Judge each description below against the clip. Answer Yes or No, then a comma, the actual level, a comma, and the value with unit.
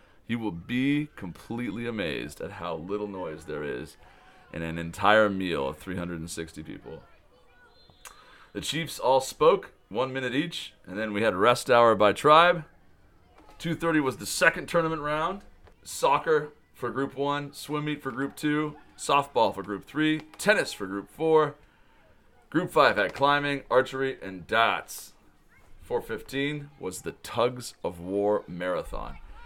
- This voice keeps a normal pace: Yes, average, 145 wpm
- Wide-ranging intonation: Yes, wide, 7.2 semitones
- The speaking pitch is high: No, low, 130 Hz